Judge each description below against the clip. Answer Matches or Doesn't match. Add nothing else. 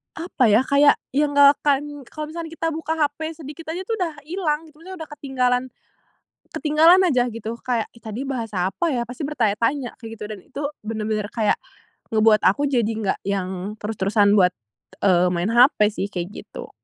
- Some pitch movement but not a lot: Doesn't match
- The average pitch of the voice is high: Matches